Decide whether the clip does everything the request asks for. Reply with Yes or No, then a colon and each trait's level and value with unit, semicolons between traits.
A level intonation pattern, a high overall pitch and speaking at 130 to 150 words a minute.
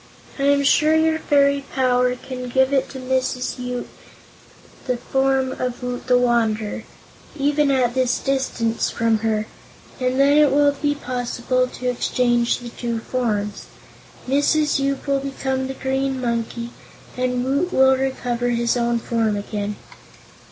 Yes: narrow, 2.3 semitones; very high, 255 Hz; average, 145 wpm